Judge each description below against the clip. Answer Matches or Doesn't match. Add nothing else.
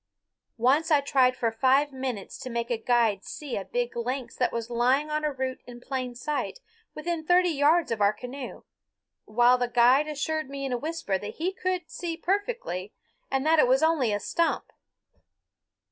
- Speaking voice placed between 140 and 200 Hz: Doesn't match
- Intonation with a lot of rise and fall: Doesn't match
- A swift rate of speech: Doesn't match